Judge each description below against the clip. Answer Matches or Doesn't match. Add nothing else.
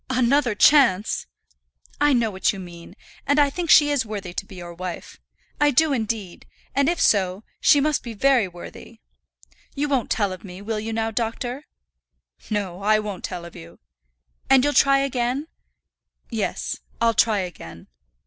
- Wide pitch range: Matches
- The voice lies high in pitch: Matches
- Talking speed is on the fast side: Doesn't match